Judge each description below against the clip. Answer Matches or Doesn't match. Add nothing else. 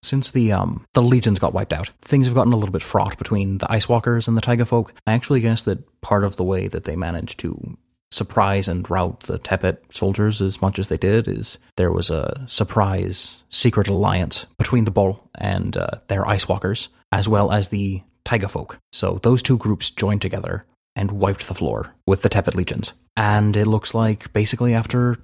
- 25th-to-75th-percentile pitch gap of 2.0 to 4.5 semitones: Matches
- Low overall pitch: Matches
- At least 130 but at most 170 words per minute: Doesn't match